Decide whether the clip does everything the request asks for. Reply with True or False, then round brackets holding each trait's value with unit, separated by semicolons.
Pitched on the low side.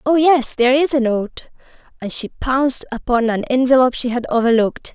False (250 Hz)